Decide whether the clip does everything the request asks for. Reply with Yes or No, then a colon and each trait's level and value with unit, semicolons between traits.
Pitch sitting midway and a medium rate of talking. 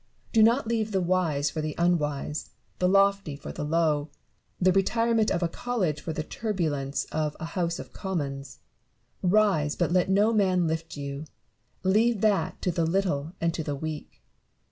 Yes: medium, 170 Hz; average, 170 wpm